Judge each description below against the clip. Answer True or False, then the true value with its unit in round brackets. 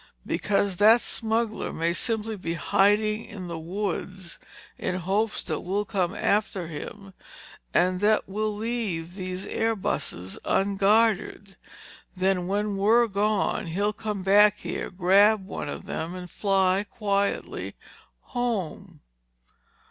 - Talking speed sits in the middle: False (120 wpm)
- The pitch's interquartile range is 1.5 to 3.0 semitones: True (2.6 semitones)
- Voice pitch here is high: True (200 Hz)